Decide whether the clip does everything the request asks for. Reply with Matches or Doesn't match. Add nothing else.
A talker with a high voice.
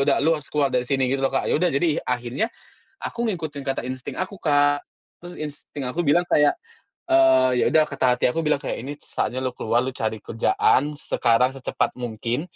Doesn't match